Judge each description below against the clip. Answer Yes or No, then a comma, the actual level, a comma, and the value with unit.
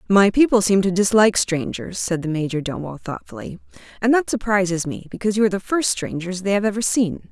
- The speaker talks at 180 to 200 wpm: Yes, average, 195 wpm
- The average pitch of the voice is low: No, high, 195 Hz